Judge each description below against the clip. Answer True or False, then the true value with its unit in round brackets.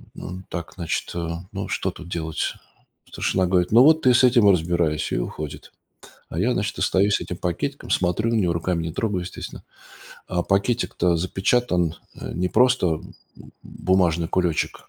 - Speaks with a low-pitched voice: True (90 Hz)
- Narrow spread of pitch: False (3.4 semitones)